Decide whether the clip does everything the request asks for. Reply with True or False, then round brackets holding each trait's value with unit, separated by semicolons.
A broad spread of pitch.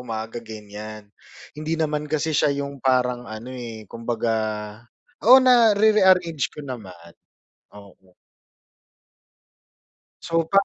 True (6.7 semitones)